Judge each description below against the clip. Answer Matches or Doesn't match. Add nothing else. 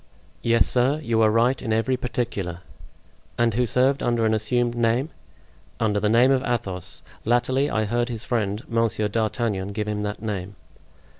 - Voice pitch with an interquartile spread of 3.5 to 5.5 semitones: Doesn't match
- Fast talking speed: Doesn't match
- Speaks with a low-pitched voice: Matches